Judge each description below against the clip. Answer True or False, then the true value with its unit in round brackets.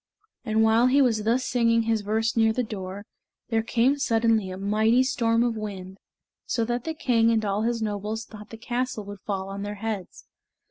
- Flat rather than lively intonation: True (2.1 semitones)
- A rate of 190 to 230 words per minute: True (195 wpm)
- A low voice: False (225 Hz)